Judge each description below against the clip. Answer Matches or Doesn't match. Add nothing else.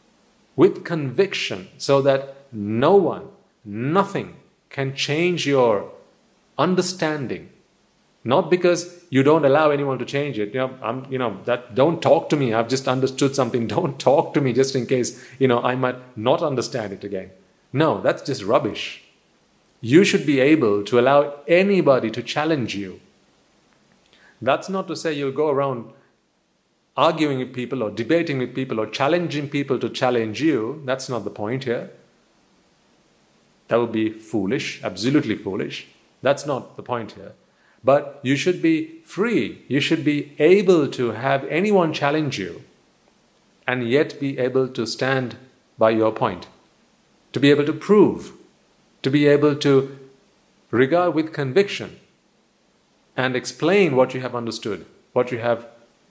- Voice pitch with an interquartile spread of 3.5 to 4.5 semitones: Matches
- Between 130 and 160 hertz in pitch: Matches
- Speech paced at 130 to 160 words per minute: Matches